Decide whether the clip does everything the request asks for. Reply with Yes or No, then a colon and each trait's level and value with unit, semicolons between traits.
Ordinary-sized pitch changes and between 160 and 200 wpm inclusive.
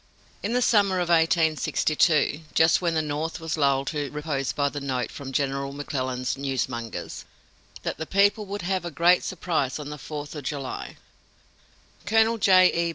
Yes: average, 4.2 semitones; average, 165 wpm